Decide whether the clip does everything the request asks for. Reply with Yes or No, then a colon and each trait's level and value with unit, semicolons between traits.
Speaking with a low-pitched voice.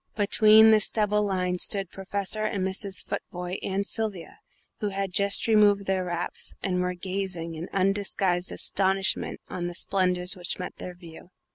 No: high, 190 Hz